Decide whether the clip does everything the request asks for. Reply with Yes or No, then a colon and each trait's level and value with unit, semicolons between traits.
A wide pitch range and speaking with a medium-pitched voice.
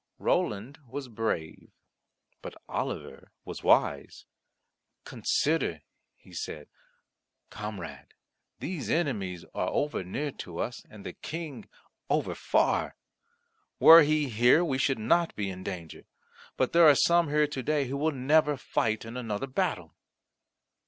No: wide, 6.2 semitones; low, 130 Hz